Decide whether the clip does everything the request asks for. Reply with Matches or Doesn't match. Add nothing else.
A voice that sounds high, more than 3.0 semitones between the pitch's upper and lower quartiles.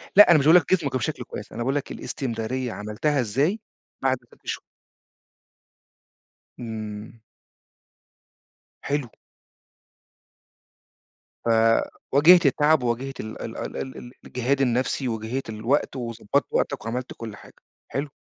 Doesn't match